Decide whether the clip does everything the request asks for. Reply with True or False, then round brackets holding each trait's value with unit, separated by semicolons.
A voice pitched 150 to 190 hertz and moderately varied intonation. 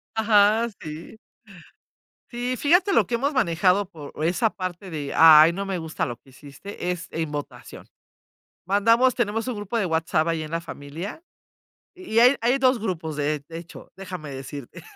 False (185 Hz; 6.3 semitones)